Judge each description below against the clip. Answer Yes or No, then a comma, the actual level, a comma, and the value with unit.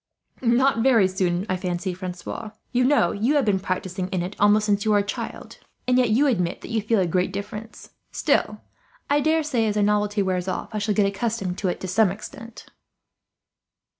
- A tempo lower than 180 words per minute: No, average, 200 wpm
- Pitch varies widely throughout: No, average, 3.5 semitones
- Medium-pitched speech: No, high, 205 Hz